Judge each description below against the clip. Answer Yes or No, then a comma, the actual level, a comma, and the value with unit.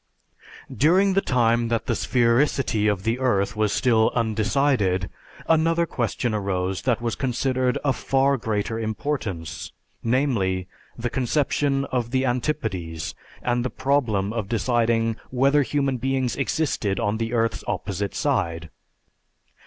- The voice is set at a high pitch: No, low, 120 Hz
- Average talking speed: No, slow, 130 wpm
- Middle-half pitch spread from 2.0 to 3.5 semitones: No, average, 4.1 semitones